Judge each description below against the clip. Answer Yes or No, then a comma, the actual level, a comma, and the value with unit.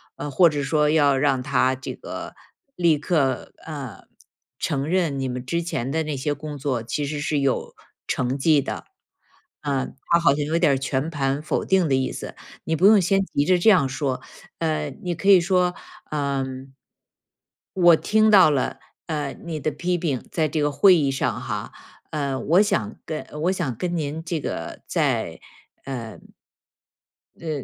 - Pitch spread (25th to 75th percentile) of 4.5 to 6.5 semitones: No, average, 3.8 semitones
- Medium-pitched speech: Yes, medium, 150 Hz